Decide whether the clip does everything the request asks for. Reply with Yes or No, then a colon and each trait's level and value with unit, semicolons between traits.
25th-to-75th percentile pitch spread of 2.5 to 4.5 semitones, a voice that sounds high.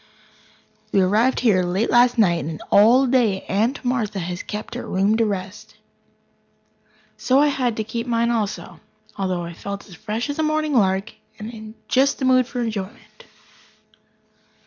Yes: average, 4.1 semitones; high, 220 Hz